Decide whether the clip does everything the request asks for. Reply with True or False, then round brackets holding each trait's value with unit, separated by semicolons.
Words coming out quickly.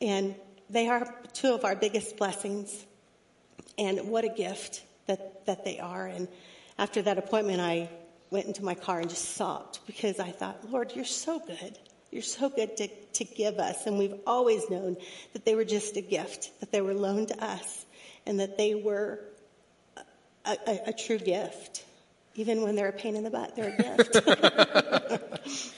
False (180 wpm)